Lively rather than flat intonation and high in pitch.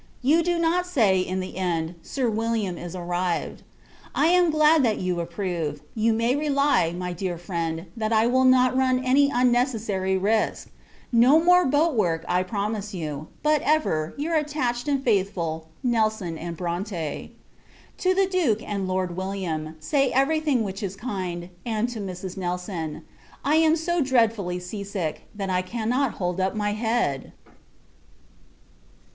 Yes: wide, 6.5 semitones; high, 210 Hz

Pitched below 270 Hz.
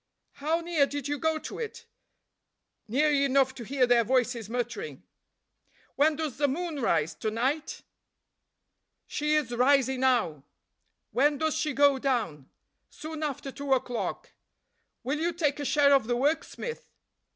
No: very high, 280 Hz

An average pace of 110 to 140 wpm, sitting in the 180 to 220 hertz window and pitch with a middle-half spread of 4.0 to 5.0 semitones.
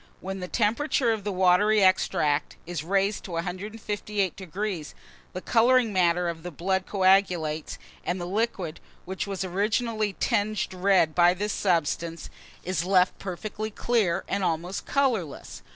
No: slow, 135 wpm; high, 190 Hz; average, 3.0 semitones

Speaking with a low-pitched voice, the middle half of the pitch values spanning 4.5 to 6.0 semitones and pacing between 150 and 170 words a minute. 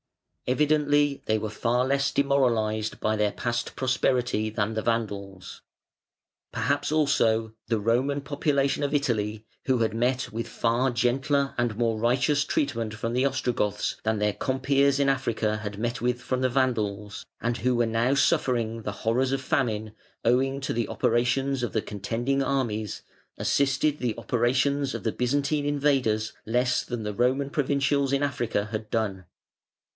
No: low, 120 Hz; average, 3.8 semitones; average, 155 wpm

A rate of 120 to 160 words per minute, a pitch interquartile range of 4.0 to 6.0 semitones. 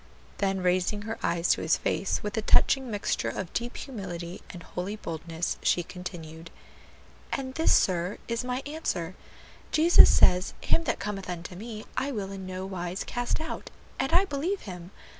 No: average, 175 wpm; wide, 5.4 semitones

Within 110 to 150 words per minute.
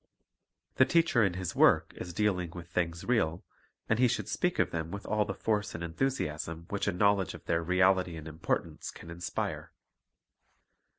No: average, 175 wpm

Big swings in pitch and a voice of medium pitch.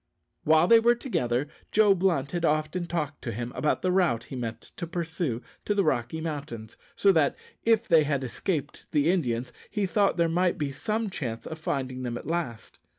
Yes: wide, 5.9 semitones; medium, 155 Hz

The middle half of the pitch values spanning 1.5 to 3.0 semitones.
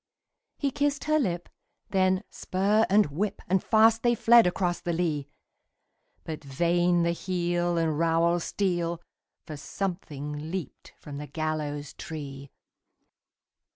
No: average, 3.7 semitones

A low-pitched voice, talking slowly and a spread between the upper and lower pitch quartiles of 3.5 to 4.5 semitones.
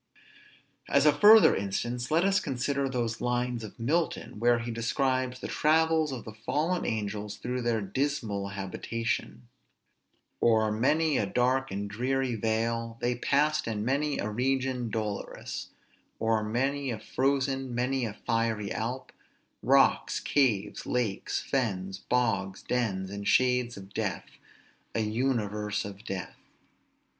Yes: low, 120 Hz; slow, 130 wpm; average, 3.8 semitones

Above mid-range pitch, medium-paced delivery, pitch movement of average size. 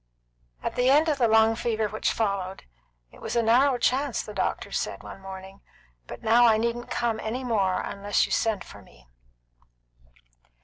Yes: high, 225 Hz; average, 175 wpm; average, 3.4 semitones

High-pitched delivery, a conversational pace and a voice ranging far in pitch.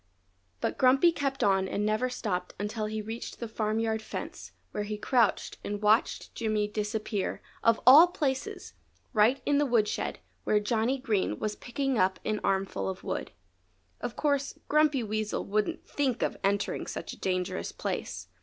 No: high, 215 Hz; average, 160 wpm; average, 3.6 semitones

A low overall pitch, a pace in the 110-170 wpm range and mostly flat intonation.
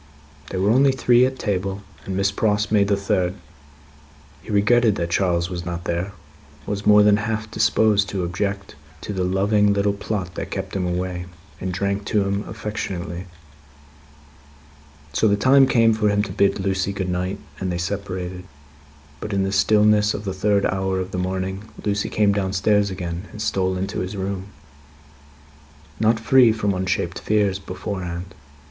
Yes: low, 100 Hz; average, 165 wpm; narrow, 2.1 semitones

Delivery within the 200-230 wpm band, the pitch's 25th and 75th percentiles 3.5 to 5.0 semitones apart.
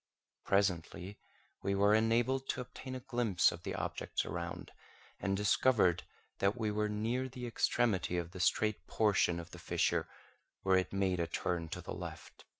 No: average, 165 wpm; average, 4.5 semitones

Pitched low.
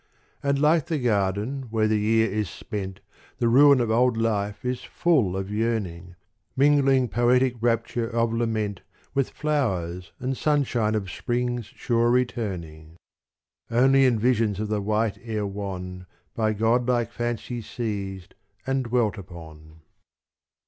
Yes: low, 115 Hz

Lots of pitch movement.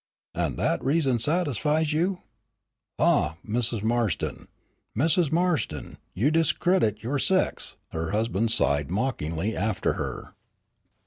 Yes: wide, 7.1 semitones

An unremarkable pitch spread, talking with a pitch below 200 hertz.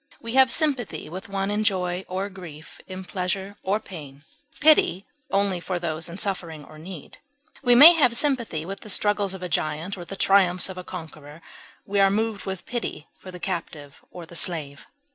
Yes: average, 3.3 semitones; high, 190 Hz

